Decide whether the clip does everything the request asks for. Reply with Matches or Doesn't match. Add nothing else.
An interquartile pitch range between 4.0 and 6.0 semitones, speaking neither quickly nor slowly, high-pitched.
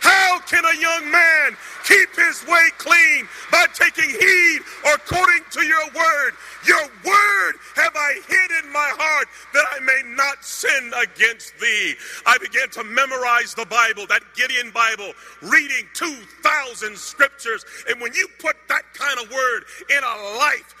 Matches